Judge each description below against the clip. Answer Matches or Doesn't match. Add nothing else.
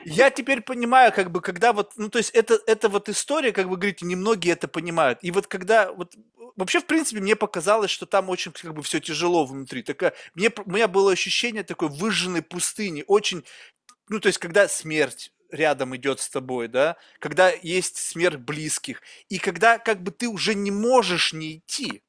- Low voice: Doesn't match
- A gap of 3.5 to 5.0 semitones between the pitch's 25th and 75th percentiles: Matches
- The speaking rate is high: Matches